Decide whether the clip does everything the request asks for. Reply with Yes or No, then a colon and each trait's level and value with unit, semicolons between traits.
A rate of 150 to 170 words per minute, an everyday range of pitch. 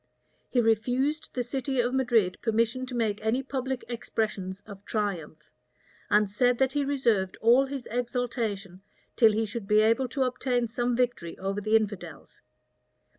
Yes: average, 160 wpm; average, 3.3 semitones